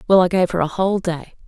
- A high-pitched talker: No, medium, 180 Hz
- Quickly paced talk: Yes, fast, 285 wpm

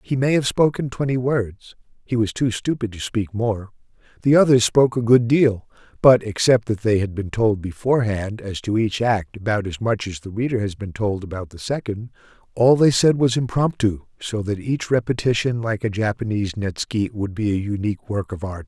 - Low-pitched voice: Yes, low, 110 Hz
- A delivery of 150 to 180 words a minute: No, average, 200 wpm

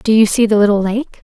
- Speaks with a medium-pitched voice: No, high, 215 Hz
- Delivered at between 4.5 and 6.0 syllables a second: Yes, 5.9 syllables/s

